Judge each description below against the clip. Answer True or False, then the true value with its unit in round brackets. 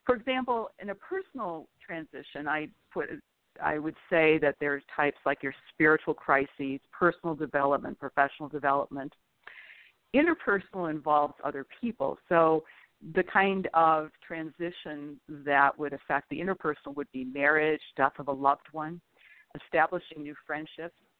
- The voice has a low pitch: False (155 Hz)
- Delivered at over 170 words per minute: False (135 wpm)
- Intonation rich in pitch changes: False (3.2 semitones)